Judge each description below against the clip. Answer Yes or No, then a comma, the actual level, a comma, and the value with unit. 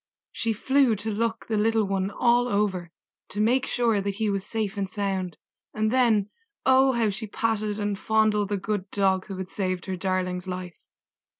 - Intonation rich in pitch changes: No, average, 2.7 semitones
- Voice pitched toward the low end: No, high, 205 Hz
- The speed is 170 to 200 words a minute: Yes, average, 185 wpm